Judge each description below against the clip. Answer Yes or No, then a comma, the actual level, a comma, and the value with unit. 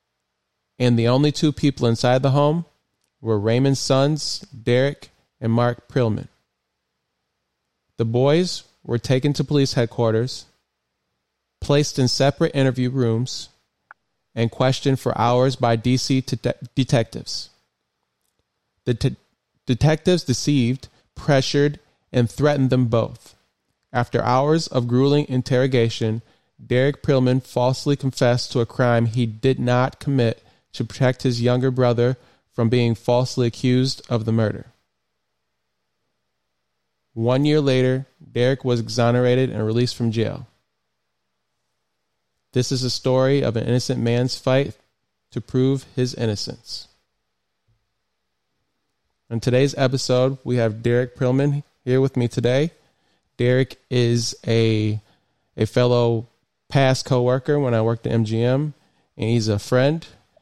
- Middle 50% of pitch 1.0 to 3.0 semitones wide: Yes, narrow, 2.6 semitones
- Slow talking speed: Yes, slow, 125 wpm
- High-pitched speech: No, low, 125 Hz